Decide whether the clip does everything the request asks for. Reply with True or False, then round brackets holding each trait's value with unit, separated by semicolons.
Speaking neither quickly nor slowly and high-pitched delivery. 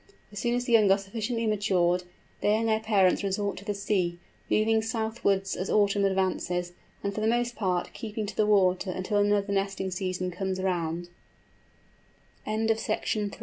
True (155 wpm; 200 Hz)